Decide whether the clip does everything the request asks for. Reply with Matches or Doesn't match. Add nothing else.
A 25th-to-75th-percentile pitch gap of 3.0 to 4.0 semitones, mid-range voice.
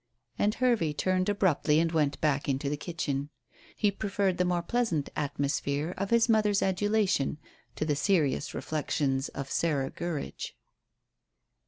Doesn't match